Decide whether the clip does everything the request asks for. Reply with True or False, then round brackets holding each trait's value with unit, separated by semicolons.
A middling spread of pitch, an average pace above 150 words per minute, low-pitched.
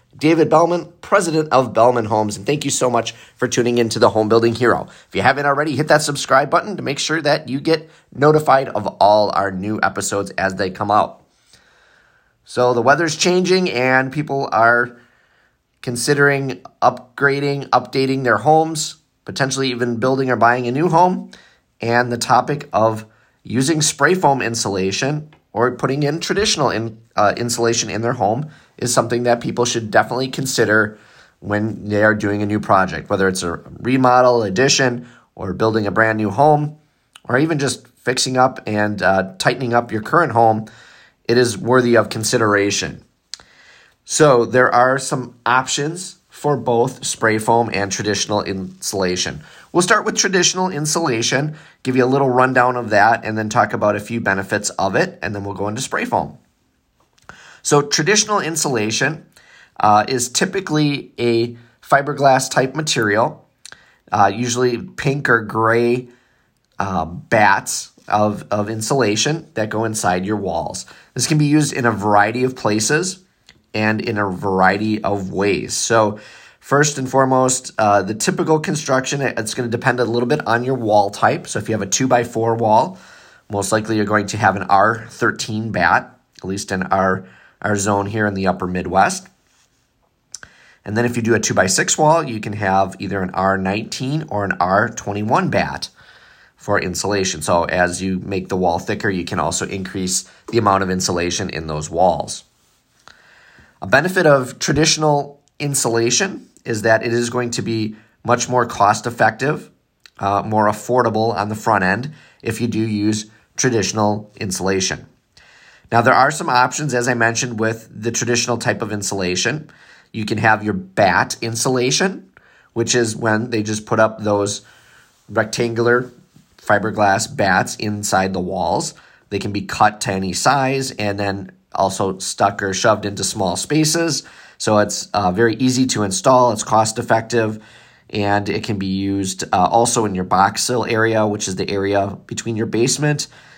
True (4.3 semitones; 165 wpm; 115 Hz)